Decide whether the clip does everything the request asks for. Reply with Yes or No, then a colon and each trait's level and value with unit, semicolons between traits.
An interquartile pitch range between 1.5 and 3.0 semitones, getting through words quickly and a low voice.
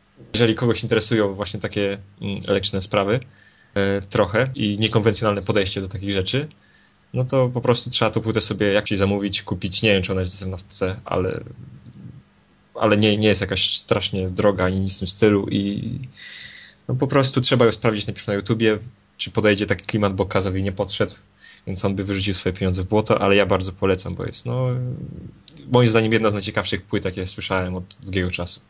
Yes: narrow, 2.5 semitones; fast, 185 wpm; low, 105 Hz